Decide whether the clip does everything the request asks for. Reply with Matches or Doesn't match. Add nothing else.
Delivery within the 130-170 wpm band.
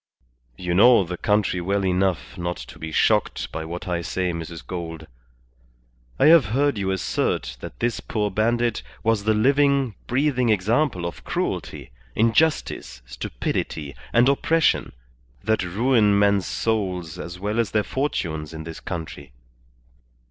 Matches